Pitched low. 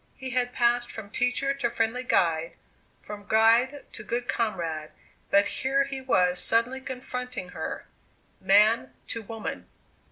No: high, 230 Hz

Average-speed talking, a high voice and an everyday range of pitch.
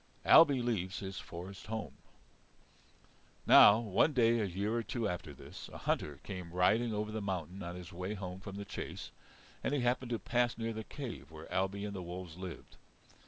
No: average, 190 wpm; low, 100 Hz; average, 4.0 semitones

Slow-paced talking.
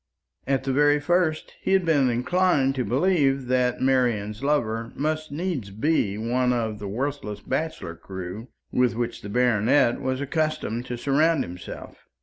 No: average, 150 wpm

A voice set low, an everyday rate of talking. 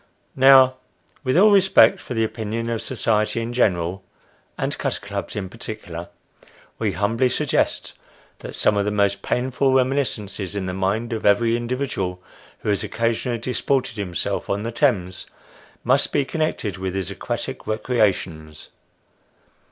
Yes: low, 110 Hz; average, 145 wpm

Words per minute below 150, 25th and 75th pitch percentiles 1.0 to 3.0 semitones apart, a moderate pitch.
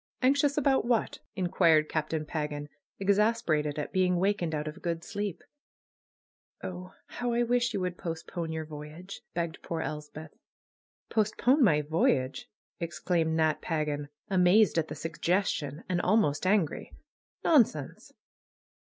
No: average, 140 wpm; average, 4.9 semitones; medium, 170 Hz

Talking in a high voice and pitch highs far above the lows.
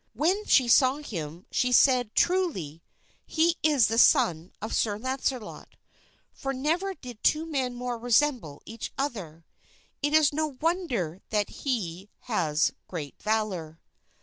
Yes: high, 245 Hz; wide, 7.4 semitones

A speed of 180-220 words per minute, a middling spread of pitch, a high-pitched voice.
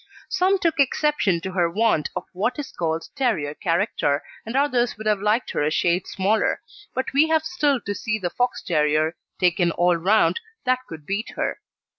No: average, 185 wpm; wide, 6.9 semitones; high, 205 Hz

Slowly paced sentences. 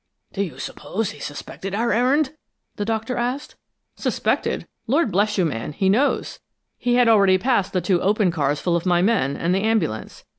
No: average, 185 wpm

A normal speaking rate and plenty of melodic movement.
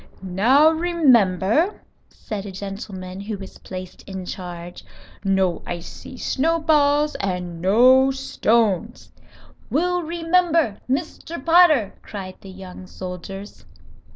No: slow, 100 wpm; wide, 8.3 semitones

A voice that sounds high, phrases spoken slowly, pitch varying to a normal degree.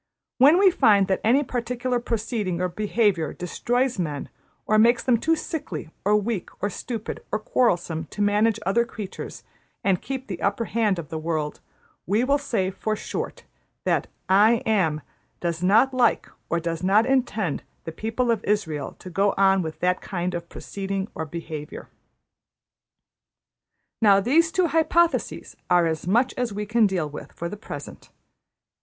No: high, 205 Hz; average, 160 wpm; average, 5.0 semitones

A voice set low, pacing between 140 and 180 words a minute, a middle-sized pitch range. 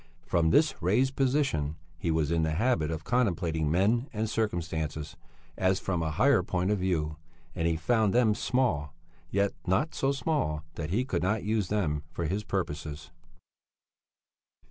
No: very low, 90 Hz; average, 160 wpm; wide, 5.8 semitones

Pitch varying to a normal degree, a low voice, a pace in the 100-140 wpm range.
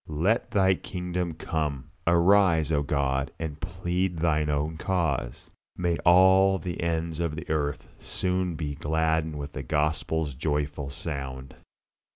Yes: average, 3.0 semitones; very low, 80 Hz; slow, 135 wpm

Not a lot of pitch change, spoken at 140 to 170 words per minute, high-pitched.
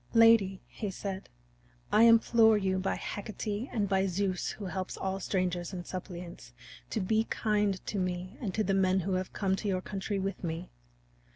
No: narrow, 2.2 semitones; average, 180 wpm; high, 195 Hz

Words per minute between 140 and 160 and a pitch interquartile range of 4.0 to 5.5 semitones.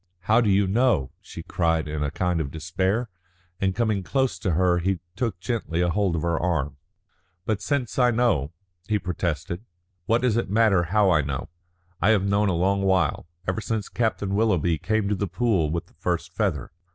No: average, 190 wpm; average, 4.4 semitones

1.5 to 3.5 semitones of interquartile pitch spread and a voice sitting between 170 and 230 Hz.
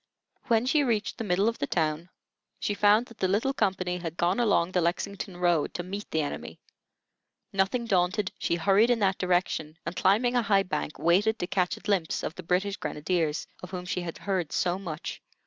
Yes: average, 3.0 semitones; medium, 185 Hz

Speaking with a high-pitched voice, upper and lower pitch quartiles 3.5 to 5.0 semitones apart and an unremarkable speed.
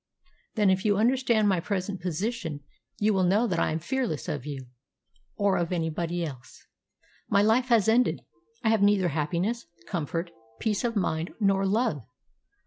Yes: high, 195 Hz; average, 4.7 semitones; average, 160 wpm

